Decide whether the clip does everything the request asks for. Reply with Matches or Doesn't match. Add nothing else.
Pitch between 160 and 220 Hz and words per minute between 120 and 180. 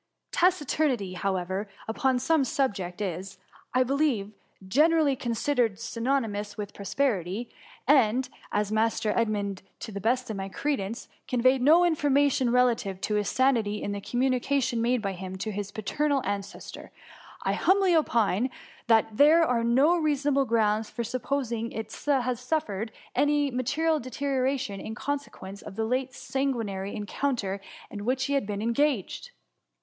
Doesn't match